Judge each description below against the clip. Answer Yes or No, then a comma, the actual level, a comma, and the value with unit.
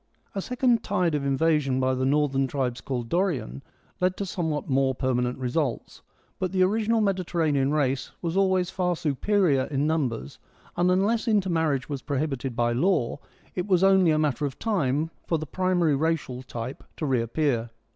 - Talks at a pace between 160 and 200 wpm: Yes, average, 170 wpm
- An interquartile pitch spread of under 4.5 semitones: No, wide, 5.6 semitones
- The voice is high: No, medium, 150 Hz